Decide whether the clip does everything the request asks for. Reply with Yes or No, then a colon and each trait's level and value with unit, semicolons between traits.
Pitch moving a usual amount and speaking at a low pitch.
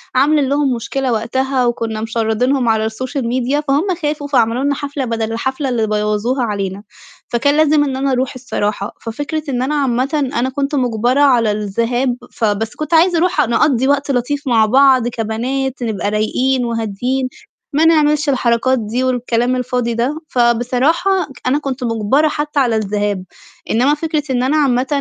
No: average, 3.5 semitones; very high, 255 Hz